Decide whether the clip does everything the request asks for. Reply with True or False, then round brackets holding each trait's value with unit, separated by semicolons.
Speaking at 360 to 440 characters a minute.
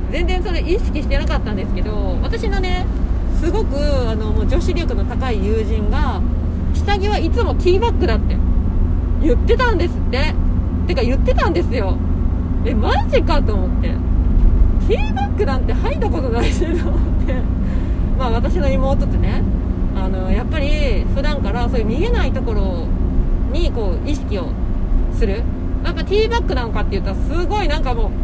False (340 characters per minute)